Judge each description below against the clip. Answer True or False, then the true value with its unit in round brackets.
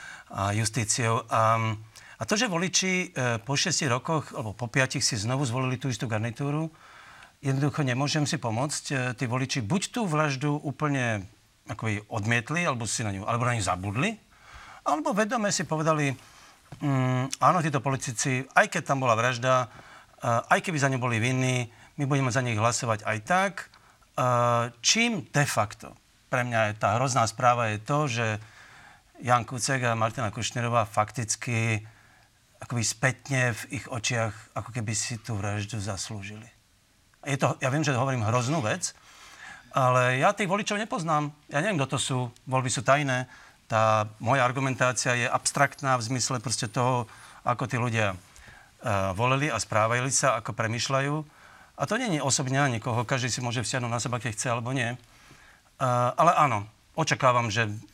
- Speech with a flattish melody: False (3.5 semitones)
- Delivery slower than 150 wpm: False (165 wpm)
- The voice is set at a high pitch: False (125 Hz)